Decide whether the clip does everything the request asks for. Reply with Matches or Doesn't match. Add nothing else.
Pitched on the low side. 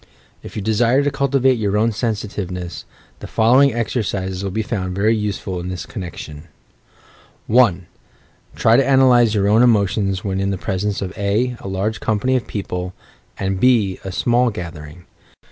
Matches